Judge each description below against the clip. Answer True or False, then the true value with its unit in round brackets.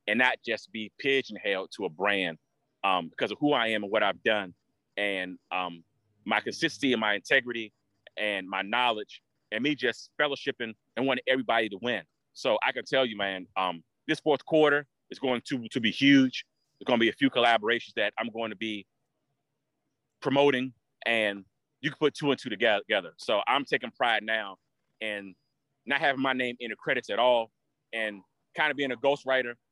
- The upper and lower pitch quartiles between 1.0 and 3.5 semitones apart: False (4.8 semitones)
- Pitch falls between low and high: False (120 Hz)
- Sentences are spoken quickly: False (190 wpm)